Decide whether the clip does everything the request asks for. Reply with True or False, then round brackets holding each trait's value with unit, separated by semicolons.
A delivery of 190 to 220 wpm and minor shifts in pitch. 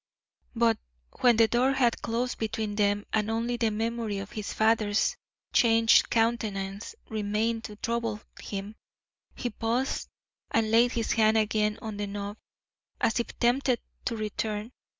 False (145 wpm; 1.8 semitones)